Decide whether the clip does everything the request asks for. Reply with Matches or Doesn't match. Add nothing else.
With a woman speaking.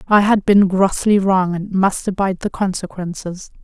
Matches